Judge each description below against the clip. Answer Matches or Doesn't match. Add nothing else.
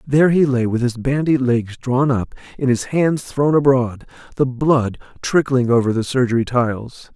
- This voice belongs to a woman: Doesn't match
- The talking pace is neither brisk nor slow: Matches